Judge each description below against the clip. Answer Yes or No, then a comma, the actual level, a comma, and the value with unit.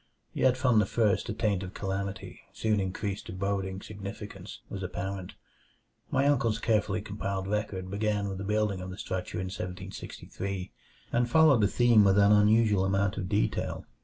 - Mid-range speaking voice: No, low, 100 Hz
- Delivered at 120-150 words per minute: No, average, 165 wpm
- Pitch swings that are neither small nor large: No, narrow, 2.0 semitones